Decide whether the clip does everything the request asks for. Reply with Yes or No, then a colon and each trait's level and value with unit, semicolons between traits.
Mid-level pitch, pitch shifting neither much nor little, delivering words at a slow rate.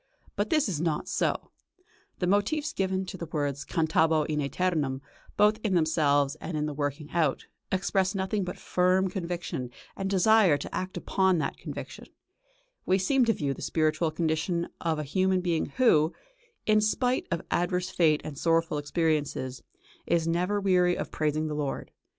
No: medium, 170 Hz; average, 3.7 semitones; average, 165 wpm